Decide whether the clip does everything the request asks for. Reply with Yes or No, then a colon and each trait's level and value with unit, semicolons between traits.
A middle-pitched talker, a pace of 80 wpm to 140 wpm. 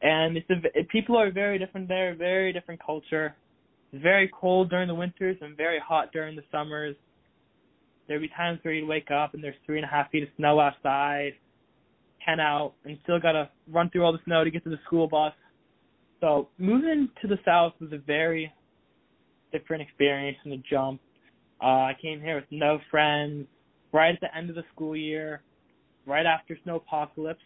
No: medium, 155 Hz; average, 195 wpm